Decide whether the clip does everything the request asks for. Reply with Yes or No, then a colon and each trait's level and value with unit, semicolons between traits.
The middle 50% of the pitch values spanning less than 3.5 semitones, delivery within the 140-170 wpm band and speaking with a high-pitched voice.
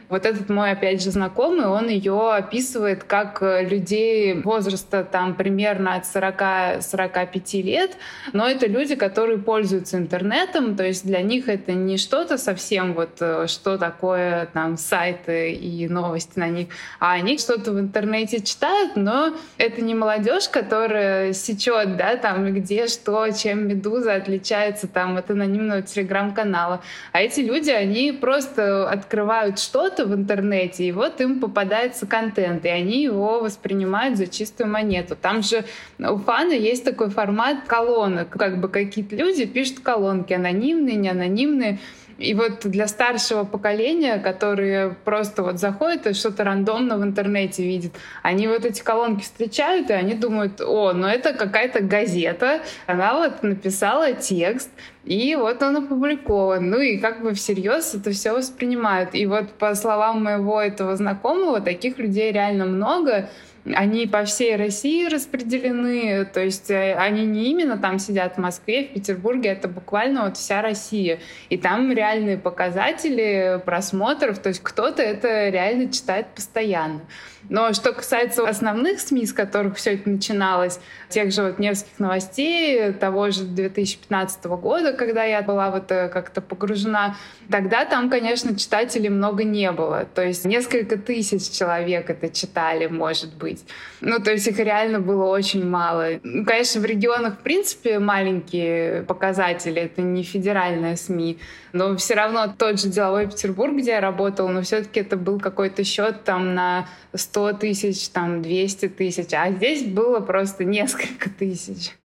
Yes: average, 3.1 semitones; average, 150 wpm; high, 205 Hz